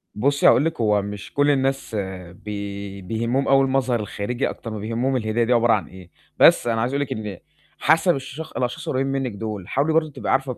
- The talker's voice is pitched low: Yes, low, 120 Hz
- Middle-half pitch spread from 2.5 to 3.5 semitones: No, average, 4.4 semitones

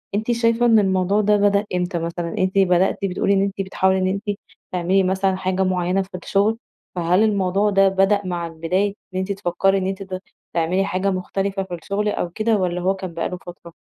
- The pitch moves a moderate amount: No, narrow, 1.7 semitones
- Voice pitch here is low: No, high, 190 Hz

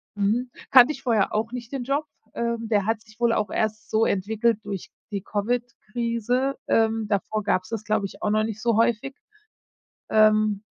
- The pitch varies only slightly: Yes, narrow, 2.0 semitones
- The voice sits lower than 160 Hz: No, high, 220 Hz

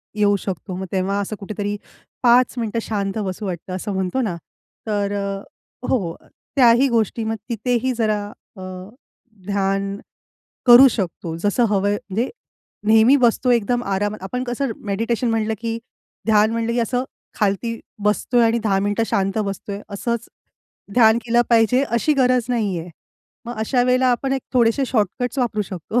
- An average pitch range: Yes, average, 3.2 semitones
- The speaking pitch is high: Yes, high, 220 Hz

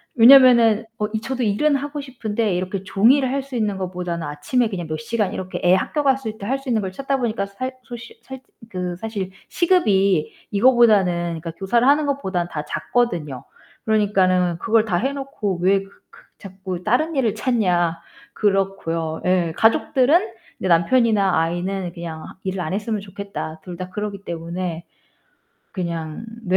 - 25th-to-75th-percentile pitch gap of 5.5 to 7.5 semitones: No, average, 5.1 semitones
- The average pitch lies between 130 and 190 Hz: No, high, 200 Hz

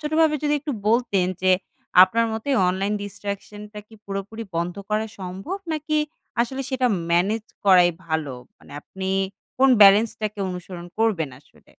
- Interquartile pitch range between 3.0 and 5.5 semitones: Yes, average, 4.1 semitones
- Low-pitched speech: No, high, 205 Hz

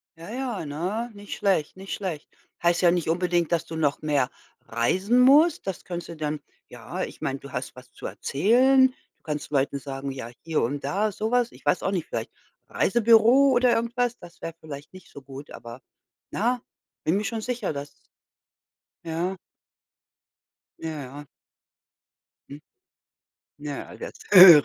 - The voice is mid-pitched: Yes, medium, 175 Hz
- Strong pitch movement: Yes, wide, 7.5 semitones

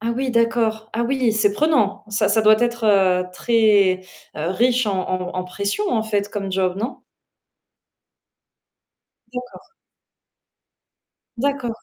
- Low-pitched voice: No, high, 220 Hz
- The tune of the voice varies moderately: Yes, average, 3.3 semitones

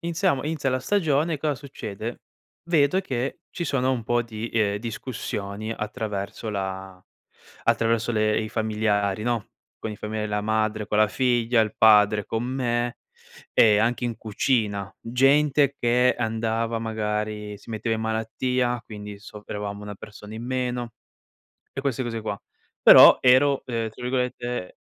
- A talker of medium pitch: No, low, 115 Hz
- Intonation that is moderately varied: Yes, average, 3.0 semitones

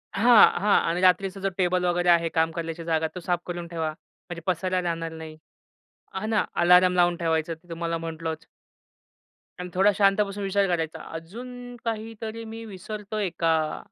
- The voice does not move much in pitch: No, average, 3.3 semitones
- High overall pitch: No, medium, 180 Hz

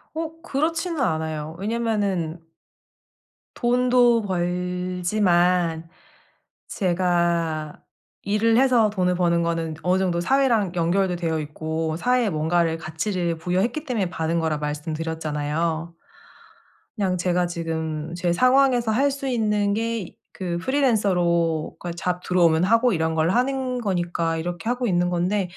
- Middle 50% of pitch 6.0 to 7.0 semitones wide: No, average, 5.2 semitones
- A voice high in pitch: No, medium, 180 Hz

